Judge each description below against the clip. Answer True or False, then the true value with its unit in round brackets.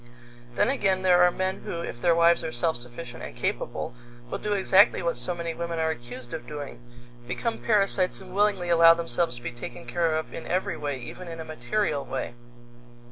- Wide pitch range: True (5.8 semitones)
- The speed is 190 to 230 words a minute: True (200 wpm)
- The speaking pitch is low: False (165 Hz)